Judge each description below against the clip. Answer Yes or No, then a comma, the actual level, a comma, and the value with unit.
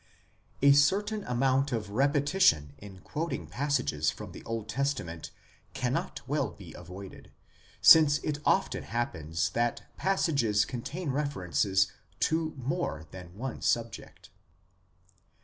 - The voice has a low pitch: Yes, low, 125 Hz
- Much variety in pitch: Yes, wide, 7.1 semitones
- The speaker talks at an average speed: No, slow, 115 wpm